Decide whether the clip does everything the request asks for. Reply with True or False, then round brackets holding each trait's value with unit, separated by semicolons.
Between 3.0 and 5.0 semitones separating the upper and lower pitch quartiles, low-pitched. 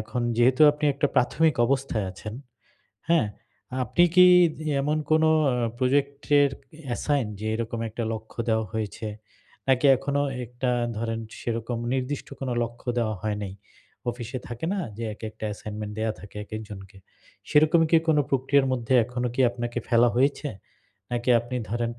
True (3.8 semitones; 120 Hz)